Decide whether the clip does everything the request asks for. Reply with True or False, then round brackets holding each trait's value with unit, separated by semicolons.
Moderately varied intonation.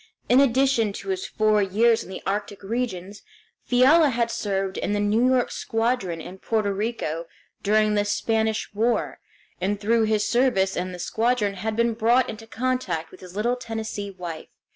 True (3.2 semitones)